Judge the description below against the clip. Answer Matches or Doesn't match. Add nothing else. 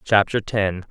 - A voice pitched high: Doesn't match